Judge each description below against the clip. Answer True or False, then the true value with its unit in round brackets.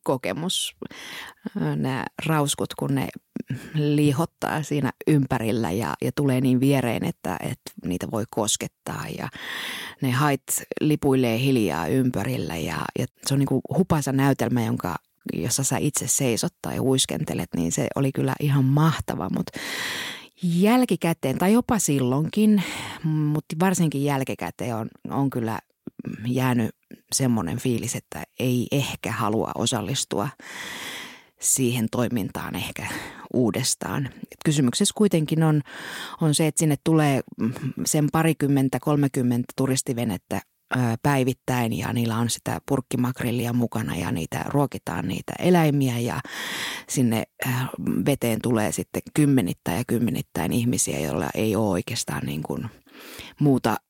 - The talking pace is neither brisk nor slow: True (120 wpm)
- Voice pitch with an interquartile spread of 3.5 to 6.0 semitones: True (4.0 semitones)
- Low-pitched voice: True (130 Hz)